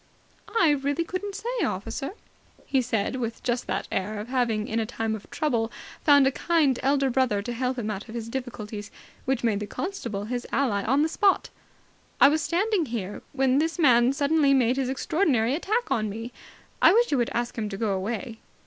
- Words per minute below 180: No, average, 200 wpm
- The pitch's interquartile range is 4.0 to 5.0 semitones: Yes, average, 4.4 semitones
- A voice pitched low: No, very high, 250 Hz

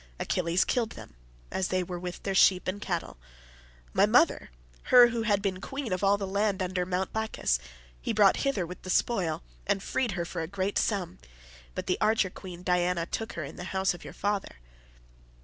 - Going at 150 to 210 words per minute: Yes, average, 190 wpm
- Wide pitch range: No, narrow, 2.5 semitones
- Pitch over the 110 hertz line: Yes, medium, 185 Hz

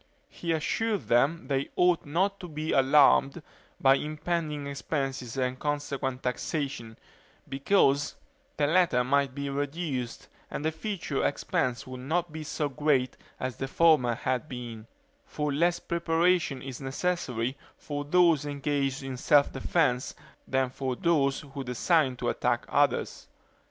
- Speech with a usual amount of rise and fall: Yes, average, 3.4 semitones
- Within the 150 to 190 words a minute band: No, slow, 135 wpm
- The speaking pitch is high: No, medium, 140 Hz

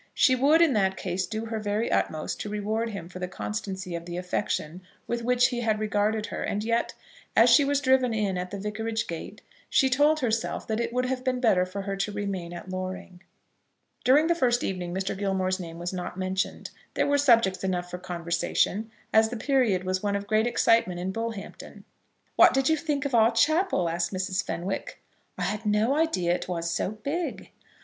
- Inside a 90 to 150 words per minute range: No, fast, 205 wpm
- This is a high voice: Yes, high, 210 Hz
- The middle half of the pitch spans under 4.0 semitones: No, average, 4.6 semitones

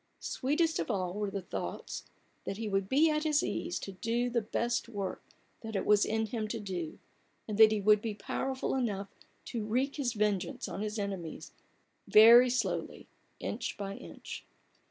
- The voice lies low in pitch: No, high, 215 Hz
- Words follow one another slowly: No, average, 175 wpm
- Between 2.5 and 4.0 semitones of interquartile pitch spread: Yes, average, 3.3 semitones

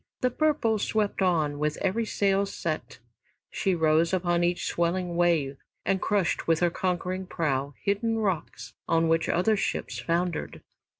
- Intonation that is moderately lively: Yes, average, 3.3 semitones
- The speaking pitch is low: No, medium, 180 Hz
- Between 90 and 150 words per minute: Yes, average, 145 wpm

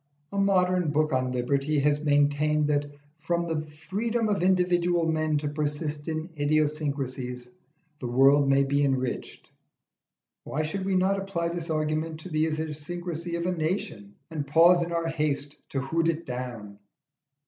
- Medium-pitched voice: Yes, medium, 155 Hz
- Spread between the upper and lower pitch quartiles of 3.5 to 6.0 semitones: No, average, 3.0 semitones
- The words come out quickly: No, average, 155 wpm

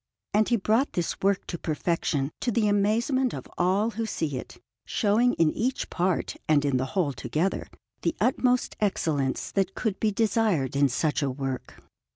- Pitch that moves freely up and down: Yes, wide, 6.9 semitones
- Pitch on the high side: Yes, high, 195 Hz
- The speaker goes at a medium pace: Yes, average, 175 wpm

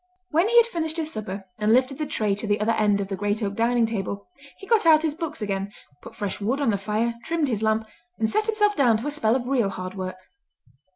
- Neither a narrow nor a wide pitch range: No, wide, 6.8 semitones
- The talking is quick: Yes, fast, 250 wpm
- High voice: Yes, high, 225 Hz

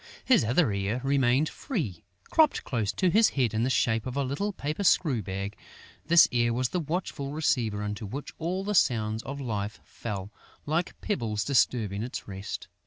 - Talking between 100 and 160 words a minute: No, average, 175 wpm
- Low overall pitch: Yes, low, 125 Hz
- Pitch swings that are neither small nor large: No, wide, 6.6 semitones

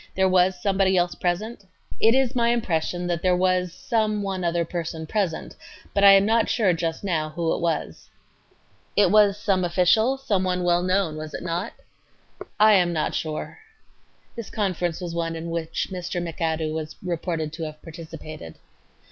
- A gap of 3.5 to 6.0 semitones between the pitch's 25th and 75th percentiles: No, average, 3.1 semitones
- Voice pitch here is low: No, medium, 180 Hz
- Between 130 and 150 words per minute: No, average, 180 wpm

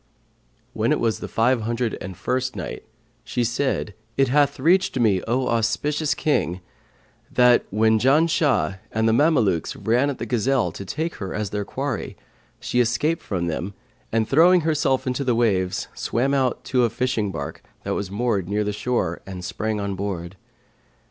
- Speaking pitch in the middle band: No, low, 115 Hz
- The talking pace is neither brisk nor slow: Yes, average, 170 wpm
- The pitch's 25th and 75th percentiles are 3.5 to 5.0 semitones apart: Yes, average, 4.7 semitones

